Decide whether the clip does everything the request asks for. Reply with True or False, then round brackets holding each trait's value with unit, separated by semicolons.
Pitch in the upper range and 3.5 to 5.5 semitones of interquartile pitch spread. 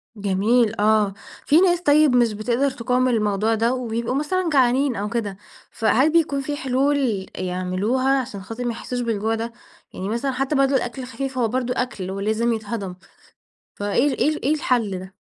True (240 Hz; 4.1 semitones)